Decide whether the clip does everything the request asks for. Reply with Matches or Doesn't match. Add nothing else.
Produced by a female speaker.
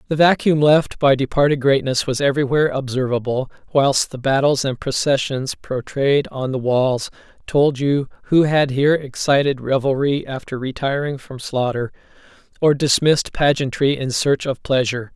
Doesn't match